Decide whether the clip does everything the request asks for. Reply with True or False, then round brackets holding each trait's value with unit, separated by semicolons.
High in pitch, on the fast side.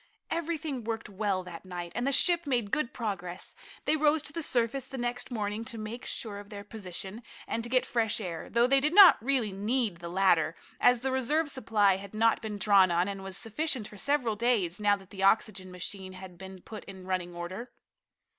True (215 Hz; 210 wpm)